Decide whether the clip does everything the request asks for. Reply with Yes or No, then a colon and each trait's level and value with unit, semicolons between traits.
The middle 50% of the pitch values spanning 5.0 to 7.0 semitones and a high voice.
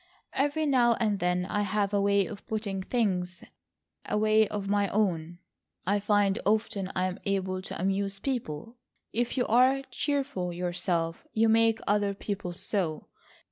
No: average, 3.2 semitones; high, 200 Hz